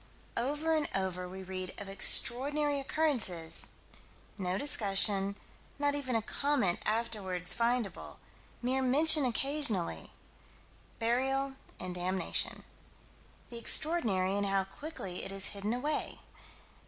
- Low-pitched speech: No, high, 230 Hz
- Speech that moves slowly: Yes, slow, 110 wpm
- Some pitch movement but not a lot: No, wide, 6.7 semitones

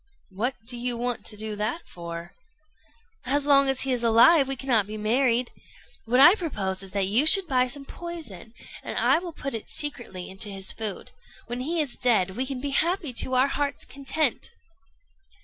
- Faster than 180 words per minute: Yes, average, 190 wpm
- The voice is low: No, very high, 250 Hz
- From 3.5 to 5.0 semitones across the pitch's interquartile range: Yes, average, 4.6 semitones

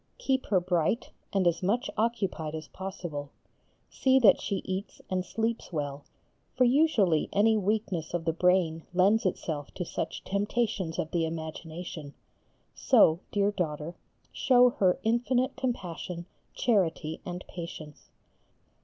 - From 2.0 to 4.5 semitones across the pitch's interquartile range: No, average, 5.3 semitones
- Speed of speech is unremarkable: No, slow, 130 wpm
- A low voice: No, medium, 185 Hz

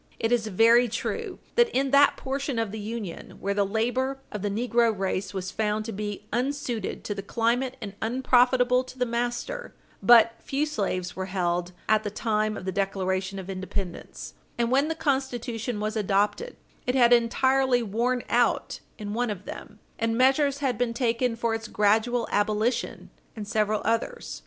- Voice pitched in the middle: No, high, 230 Hz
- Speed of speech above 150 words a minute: Yes, average, 175 wpm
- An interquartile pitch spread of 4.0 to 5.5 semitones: No, average, 3.3 semitones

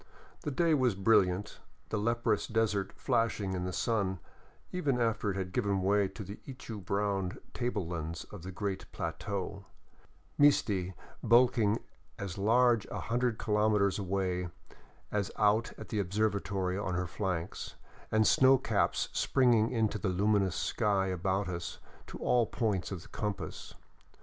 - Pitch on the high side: No, low, 100 Hz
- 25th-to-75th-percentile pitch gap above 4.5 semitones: No, average, 3.2 semitones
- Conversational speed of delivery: Yes, average, 145 wpm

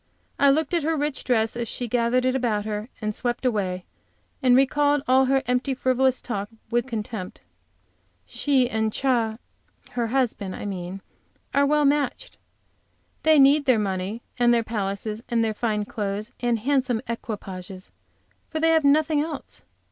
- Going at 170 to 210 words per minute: No, average, 160 wpm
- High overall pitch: Yes, high, 240 Hz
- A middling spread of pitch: Yes, average, 4.2 semitones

